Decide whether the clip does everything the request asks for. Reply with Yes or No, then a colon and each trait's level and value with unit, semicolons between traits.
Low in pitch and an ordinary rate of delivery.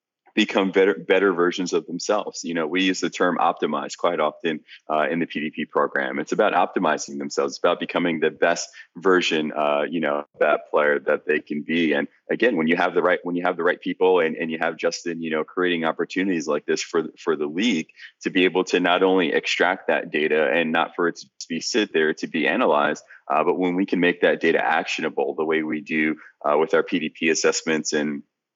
No: very low, 80 Hz; fast, 225 wpm